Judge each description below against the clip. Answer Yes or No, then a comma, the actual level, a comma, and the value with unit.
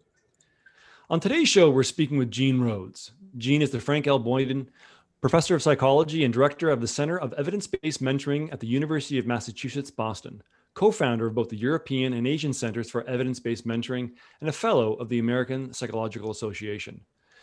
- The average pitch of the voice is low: Yes, low, 130 Hz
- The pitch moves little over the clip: No, average, 3.5 semitones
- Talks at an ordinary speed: Yes, average, 185 wpm